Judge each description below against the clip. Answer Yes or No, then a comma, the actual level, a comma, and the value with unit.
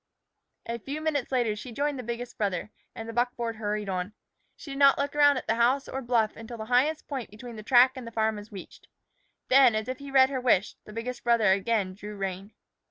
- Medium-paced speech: No, fast, 230 wpm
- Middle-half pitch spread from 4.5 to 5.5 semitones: No, average, 3.6 semitones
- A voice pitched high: Yes, high, 235 Hz